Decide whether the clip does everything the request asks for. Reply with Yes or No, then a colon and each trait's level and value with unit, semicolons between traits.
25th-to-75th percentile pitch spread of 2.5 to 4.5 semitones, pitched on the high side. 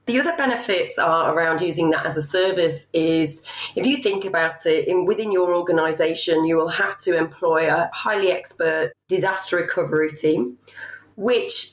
No: average, 3.8 semitones; medium, 170 Hz